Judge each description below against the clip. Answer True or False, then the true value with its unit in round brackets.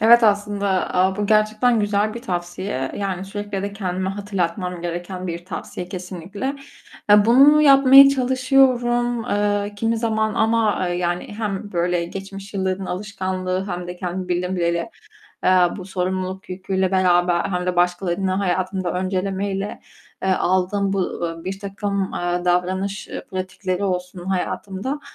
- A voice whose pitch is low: False (190 Hz)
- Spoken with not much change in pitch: True (2.3 semitones)